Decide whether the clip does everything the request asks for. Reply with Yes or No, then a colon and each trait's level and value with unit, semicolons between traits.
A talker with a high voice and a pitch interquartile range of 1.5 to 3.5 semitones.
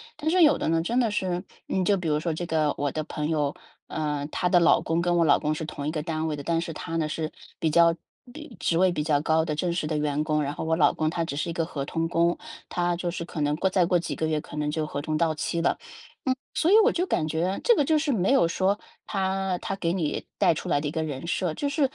No: medium, 165 Hz; average, 2.9 semitones